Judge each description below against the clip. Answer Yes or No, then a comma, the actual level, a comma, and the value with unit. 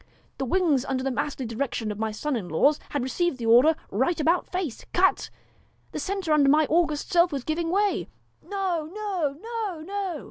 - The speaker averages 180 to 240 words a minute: Yes, average, 200 wpm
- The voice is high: Yes, very high, 310 Hz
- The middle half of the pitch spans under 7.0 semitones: Yes, wide, 5.6 semitones